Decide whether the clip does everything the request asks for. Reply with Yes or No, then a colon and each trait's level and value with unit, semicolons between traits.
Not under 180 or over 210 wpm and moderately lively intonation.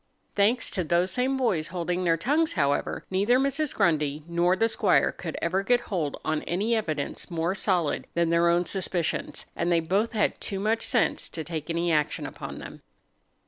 Yes: average, 185 wpm; average, 4.8 semitones